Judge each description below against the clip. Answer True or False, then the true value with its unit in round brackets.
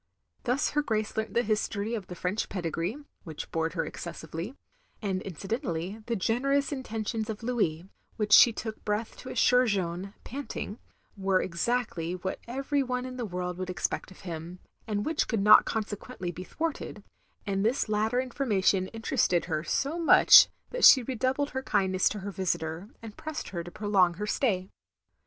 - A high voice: True (210 Hz)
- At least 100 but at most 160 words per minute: False (170 wpm)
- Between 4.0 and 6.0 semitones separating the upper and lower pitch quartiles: True (5.1 semitones)